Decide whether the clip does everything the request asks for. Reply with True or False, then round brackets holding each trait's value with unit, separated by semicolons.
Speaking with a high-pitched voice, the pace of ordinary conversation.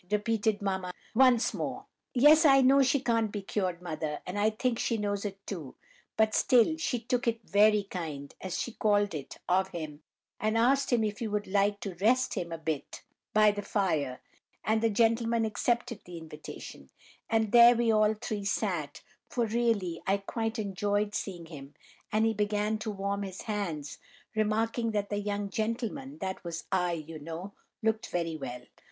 True (210 Hz; 175 wpm)